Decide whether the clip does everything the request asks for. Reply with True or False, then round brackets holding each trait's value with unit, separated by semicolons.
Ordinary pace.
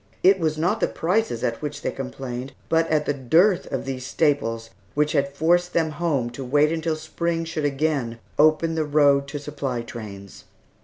True (185 wpm)